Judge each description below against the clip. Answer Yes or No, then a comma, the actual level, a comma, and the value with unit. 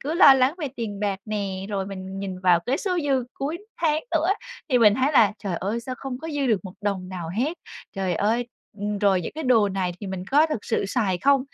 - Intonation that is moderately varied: No, wide, 6.0 semitones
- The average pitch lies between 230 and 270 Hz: No, high, 215 Hz